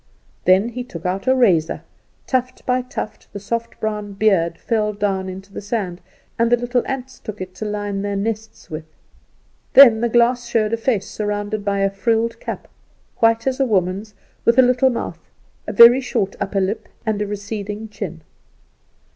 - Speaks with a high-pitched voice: Yes, high, 215 Hz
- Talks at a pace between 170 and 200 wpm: Yes, average, 180 wpm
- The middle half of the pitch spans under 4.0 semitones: Yes, average, 3.1 semitones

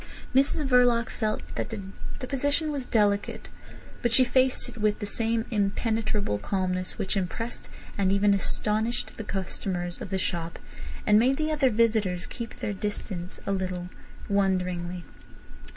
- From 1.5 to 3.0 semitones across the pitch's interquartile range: No, average, 4.0 semitones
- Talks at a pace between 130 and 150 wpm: Yes, average, 145 wpm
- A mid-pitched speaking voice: No, high, 210 Hz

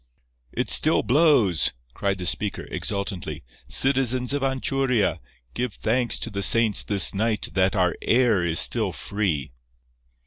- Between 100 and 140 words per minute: Yes, slow, 135 wpm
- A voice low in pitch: Yes, low, 110 Hz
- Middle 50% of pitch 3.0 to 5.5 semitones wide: Yes, average, 4.6 semitones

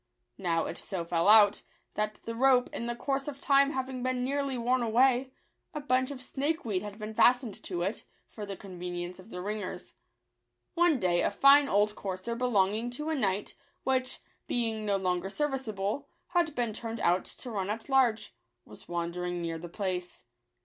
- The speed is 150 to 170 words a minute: No, average, 180 wpm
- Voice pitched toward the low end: No, high, 220 Hz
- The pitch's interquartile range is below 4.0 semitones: No, wide, 5.4 semitones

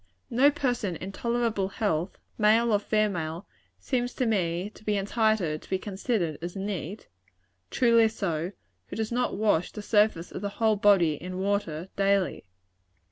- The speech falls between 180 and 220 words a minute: No, average, 155 wpm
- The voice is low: No, high, 205 Hz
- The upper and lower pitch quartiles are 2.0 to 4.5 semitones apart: Yes, average, 3.5 semitones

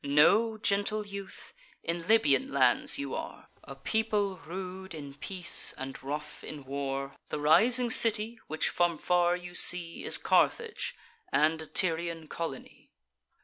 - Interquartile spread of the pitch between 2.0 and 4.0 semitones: No, average, 5.2 semitones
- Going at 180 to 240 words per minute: No, average, 140 wpm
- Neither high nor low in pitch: Yes, medium, 170 Hz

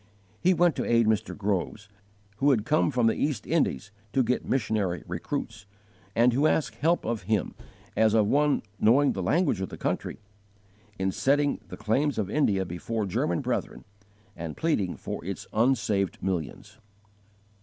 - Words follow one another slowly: No, average, 160 wpm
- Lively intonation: Yes, wide, 6.2 semitones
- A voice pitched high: No, low, 110 Hz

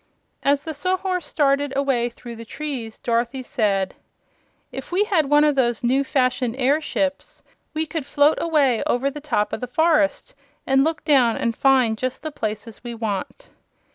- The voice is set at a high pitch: Yes, very high, 270 Hz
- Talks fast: No, average, 170 wpm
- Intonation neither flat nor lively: Yes, average, 4.0 semitones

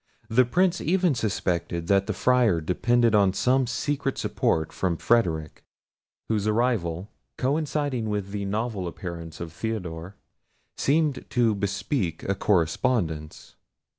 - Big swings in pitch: Yes, wide, 6.4 semitones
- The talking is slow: Yes, slow, 120 wpm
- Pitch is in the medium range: No, low, 105 Hz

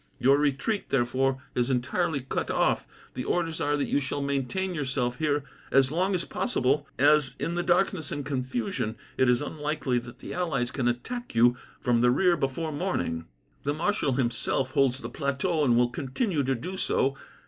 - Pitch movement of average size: Yes, average, 4.3 semitones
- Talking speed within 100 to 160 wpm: No, average, 180 wpm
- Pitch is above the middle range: No, medium, 140 Hz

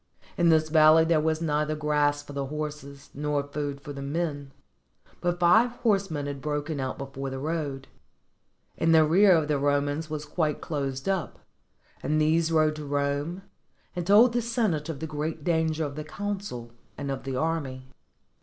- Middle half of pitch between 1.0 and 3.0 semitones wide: Yes, narrow, 2.4 semitones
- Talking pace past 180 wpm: No, average, 175 wpm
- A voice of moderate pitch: Yes, medium, 150 Hz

